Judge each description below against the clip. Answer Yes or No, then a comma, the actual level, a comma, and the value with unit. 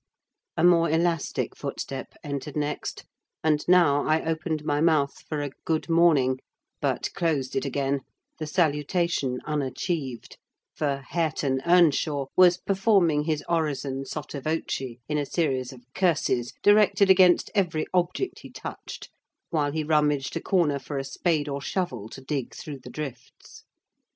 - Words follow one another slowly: No, average, 145 wpm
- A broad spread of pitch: No, average, 3.6 semitones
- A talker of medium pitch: Yes, medium, 150 Hz